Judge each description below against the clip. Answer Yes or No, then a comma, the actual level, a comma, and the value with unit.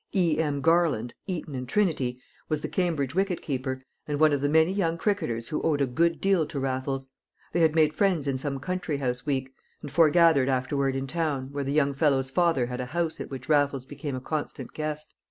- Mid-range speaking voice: Yes, medium, 145 Hz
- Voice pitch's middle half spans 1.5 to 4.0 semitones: Yes, average, 3.6 semitones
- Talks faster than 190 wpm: Yes, fast, 205 wpm